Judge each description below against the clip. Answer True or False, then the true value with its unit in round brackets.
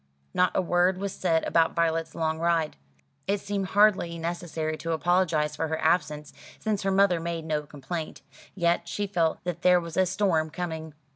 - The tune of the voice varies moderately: False (2.2 semitones)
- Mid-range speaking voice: True (170 Hz)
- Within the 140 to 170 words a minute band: False (180 wpm)